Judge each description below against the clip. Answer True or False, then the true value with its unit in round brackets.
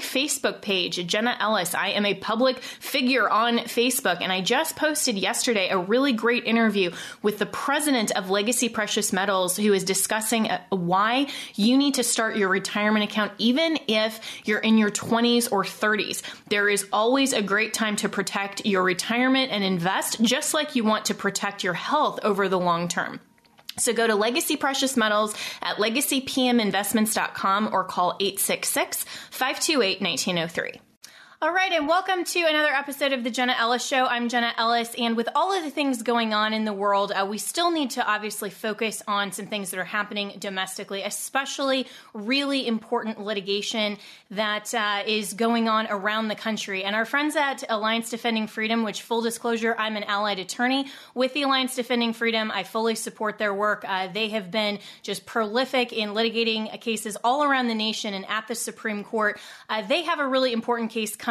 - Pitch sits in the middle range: False (220 Hz)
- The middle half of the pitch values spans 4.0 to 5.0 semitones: False (3.3 semitones)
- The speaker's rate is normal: True (180 wpm)